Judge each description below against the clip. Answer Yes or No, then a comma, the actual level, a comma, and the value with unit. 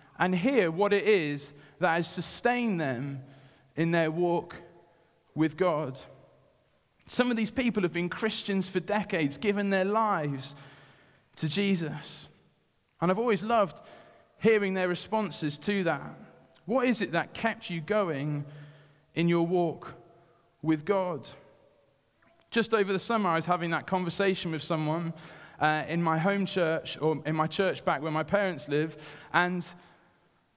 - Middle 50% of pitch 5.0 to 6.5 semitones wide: No, average, 4.2 semitones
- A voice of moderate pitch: Yes, medium, 170 Hz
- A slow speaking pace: No, average, 145 wpm